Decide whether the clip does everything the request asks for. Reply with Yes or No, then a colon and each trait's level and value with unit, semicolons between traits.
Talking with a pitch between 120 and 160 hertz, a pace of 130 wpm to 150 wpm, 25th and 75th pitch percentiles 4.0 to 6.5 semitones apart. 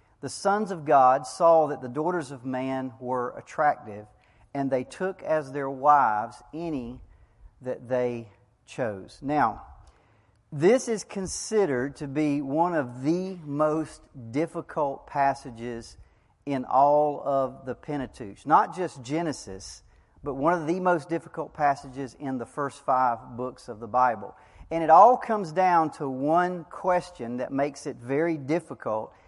Yes: medium, 140 Hz; average, 145 wpm; average, 4.6 semitones